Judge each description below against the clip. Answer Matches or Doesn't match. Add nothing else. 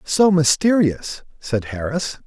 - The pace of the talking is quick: Doesn't match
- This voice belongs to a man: Matches